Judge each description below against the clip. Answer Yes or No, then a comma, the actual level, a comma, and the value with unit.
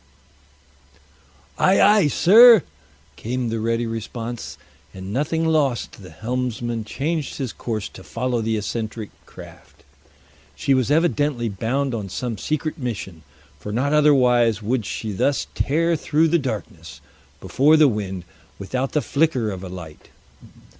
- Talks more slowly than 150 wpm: Yes, slow, 135 wpm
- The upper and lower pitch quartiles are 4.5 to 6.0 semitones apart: Yes, average, 5.2 semitones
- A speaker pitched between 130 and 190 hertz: No, low, 120 Hz